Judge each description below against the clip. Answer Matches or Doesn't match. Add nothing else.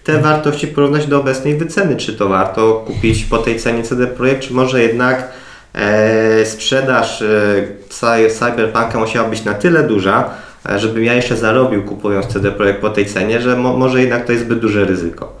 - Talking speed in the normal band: Doesn't match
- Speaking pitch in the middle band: Doesn't match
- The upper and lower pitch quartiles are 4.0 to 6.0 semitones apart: Doesn't match